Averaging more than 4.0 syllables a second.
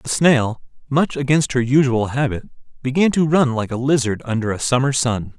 Yes: 5.1 syllables/s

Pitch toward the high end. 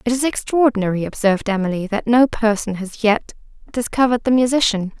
Yes: high, 225 Hz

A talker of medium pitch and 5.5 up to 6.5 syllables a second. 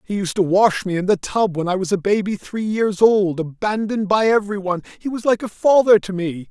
No: high, 200 Hz; 5.6 syllables/s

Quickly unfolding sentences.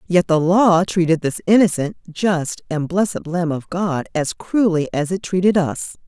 No: average, 180 wpm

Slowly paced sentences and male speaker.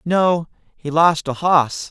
No: average, 155 wpm; male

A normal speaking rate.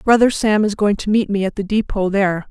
No: fast, 265 wpm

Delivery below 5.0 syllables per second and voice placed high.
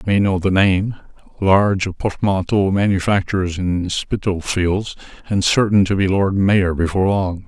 No: 4.6 syllables/s; very low, 95 Hz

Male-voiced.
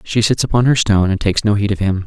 Yes: male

